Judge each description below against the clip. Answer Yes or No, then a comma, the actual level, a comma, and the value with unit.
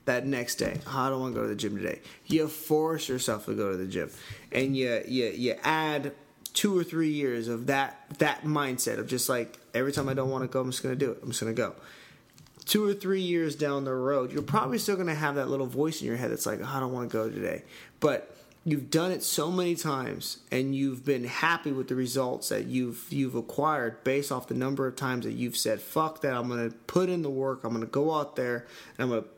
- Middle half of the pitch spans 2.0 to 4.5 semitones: Yes, average, 3.5 semitones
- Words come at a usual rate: No, fast, 250 wpm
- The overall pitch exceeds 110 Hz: Yes, low, 135 Hz